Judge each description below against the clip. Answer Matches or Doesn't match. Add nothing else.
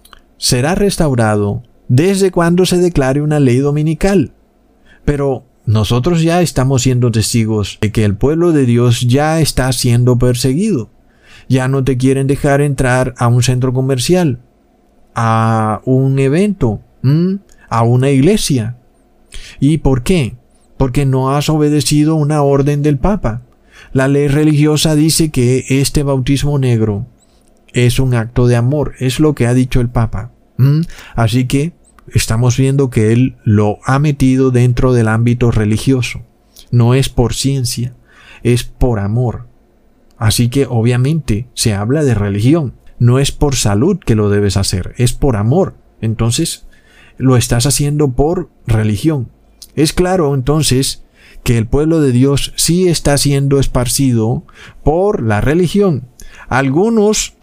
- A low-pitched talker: Matches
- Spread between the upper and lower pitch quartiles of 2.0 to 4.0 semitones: Matches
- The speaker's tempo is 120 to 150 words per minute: Matches